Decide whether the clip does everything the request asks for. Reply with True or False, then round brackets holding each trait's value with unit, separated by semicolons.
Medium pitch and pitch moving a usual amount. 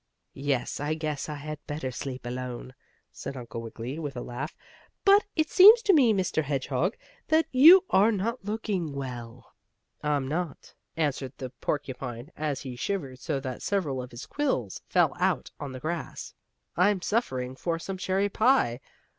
False (150 Hz; 7.4 semitones)